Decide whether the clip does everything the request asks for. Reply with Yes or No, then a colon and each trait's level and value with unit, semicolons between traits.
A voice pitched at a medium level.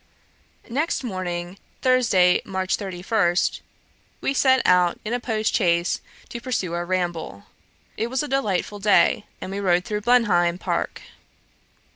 No: high, 195 Hz